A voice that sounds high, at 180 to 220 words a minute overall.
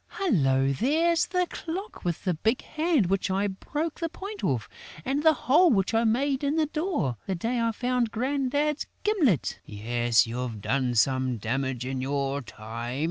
No: high, 215 Hz; average, 170 wpm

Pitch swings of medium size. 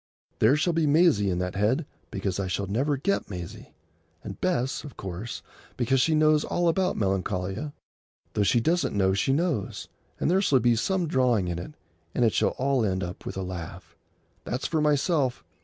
No: wide, 8.0 semitones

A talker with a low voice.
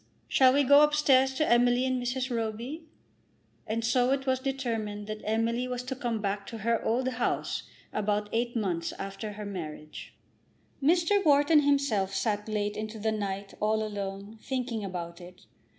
No: high, 230 Hz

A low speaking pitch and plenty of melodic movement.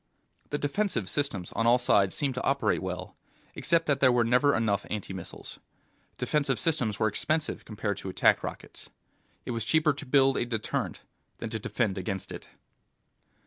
Yes: low, 120 Hz; wide, 5.8 semitones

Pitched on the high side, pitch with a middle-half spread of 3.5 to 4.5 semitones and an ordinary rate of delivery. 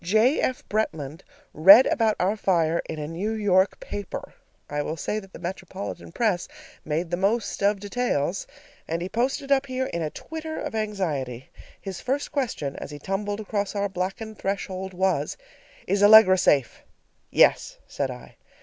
Yes: high, 195 Hz; average, 4.2 semitones; average, 165 wpm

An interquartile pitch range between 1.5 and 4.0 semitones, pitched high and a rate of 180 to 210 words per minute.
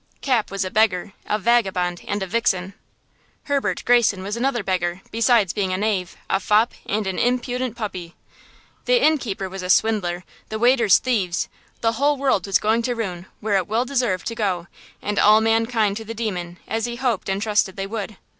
Yes: average, 3.6 semitones; high, 215 Hz; average, 185 wpm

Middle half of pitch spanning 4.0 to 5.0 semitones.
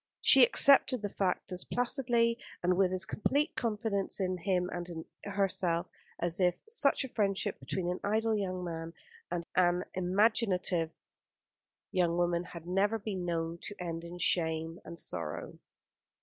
No: average, 3.2 semitones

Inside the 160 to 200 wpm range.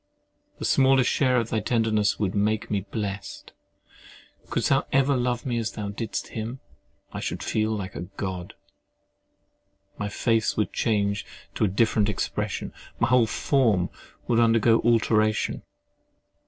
No: average, 145 wpm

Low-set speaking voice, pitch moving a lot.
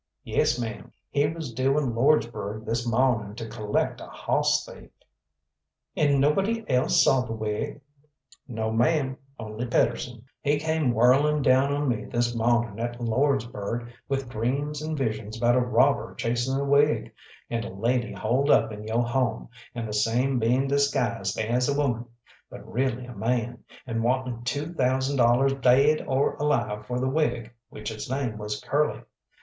No: low, 125 Hz; average, 3.3 semitones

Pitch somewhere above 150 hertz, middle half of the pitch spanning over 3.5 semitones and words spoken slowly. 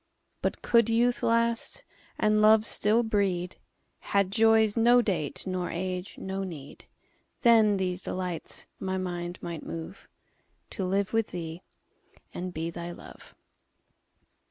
Yes: high, 190 Hz; average, 3.9 semitones; slow, 115 wpm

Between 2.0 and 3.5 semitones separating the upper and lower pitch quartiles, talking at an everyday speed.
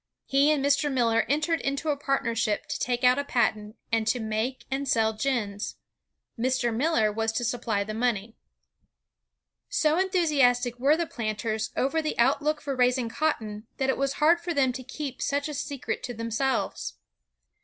No: average, 3.9 semitones; average, 170 wpm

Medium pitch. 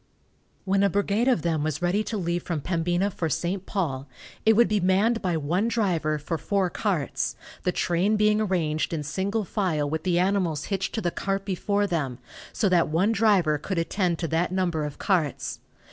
Yes: medium, 180 Hz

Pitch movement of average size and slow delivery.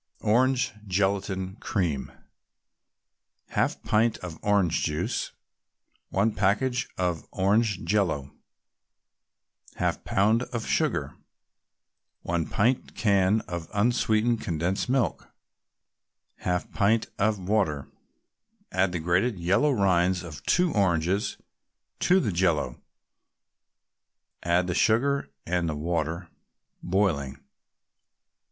Yes: average, 4.1 semitones; slow, 95 wpm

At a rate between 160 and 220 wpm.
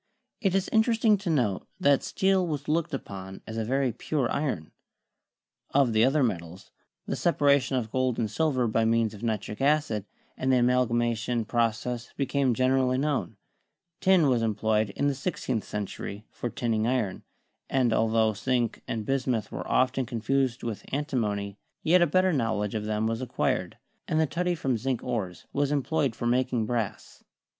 Yes: average, 165 wpm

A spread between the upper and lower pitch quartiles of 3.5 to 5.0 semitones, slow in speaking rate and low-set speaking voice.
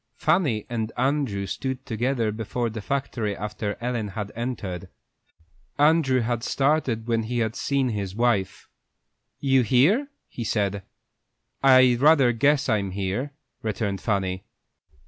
Yes: average, 4.1 semitones; slow, 125 wpm; low, 120 Hz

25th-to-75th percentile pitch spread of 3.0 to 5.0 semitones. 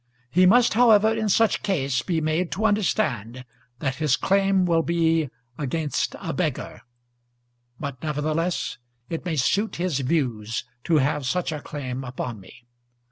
No: wide, 5.6 semitones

